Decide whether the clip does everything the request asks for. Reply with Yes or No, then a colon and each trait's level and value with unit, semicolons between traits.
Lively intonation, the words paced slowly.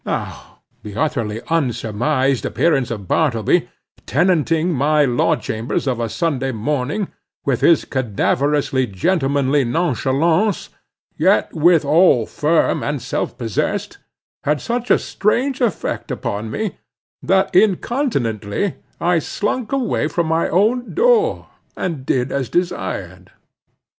Yes: wide, 6.5 semitones; slow, 115 wpm